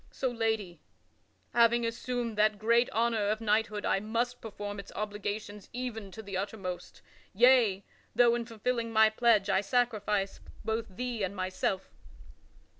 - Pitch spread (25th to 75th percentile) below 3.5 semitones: Yes, narrow, 2.5 semitones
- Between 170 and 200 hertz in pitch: No, high, 220 Hz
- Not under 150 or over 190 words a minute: No, average, 140 wpm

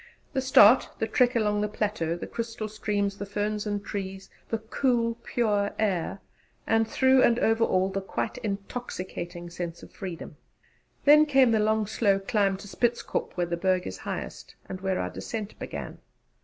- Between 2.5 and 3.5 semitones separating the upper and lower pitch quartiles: Yes, average, 2.9 semitones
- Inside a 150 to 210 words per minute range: Yes, average, 170 wpm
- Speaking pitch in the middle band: No, high, 210 Hz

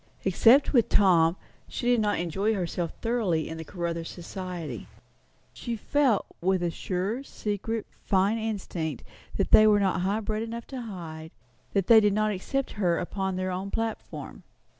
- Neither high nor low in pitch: No, high, 195 Hz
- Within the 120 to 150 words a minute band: No, average, 165 wpm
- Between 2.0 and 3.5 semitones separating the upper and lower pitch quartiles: No, average, 4.0 semitones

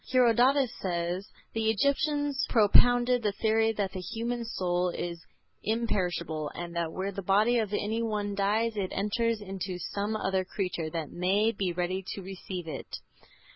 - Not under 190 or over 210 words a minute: No, average, 155 wpm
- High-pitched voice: Yes, high, 200 Hz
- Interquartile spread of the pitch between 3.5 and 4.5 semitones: Yes, average, 3.9 semitones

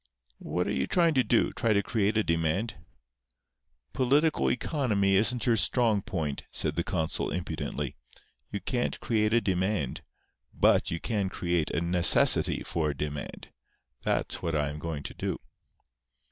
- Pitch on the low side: Yes, very low, 95 Hz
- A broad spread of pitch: Yes, wide, 6.0 semitones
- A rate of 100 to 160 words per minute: Yes, average, 150 wpm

